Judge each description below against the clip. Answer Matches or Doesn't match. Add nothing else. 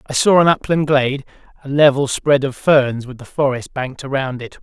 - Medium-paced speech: Doesn't match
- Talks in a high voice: Doesn't match